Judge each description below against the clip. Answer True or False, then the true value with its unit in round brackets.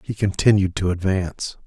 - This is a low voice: True (95 Hz)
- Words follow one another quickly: False (145 wpm)